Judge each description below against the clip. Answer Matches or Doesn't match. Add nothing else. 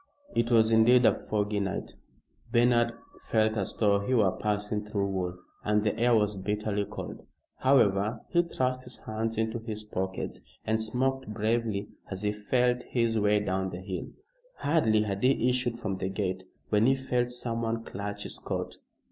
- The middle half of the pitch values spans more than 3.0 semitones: Doesn't match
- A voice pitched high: Doesn't match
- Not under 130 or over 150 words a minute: Doesn't match